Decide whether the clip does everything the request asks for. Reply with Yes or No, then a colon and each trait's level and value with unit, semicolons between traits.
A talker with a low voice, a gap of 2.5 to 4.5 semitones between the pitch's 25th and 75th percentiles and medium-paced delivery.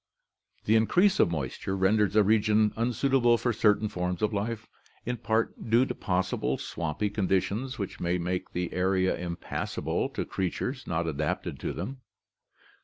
Yes: low, 105 Hz; average, 4.1 semitones; average, 150 wpm